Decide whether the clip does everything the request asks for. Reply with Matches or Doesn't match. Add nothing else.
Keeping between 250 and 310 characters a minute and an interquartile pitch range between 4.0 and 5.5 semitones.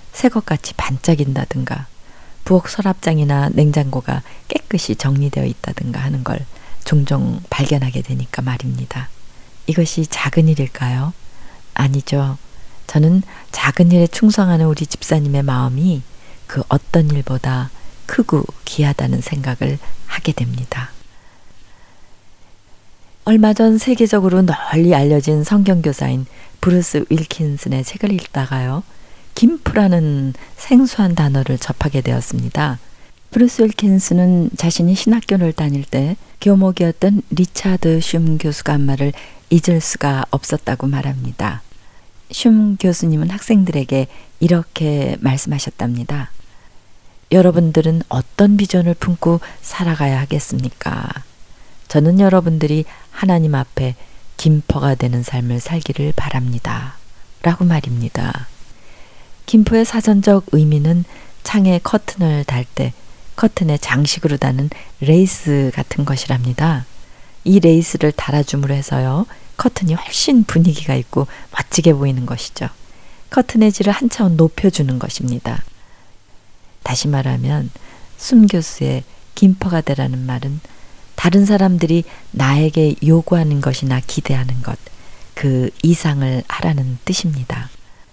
Matches